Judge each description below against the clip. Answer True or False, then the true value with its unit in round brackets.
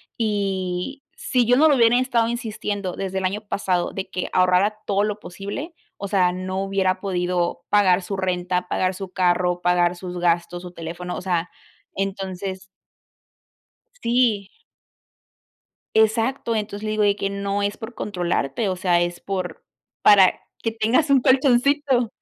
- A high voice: True (195 Hz)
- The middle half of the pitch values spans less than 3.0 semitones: False (3.3 semitones)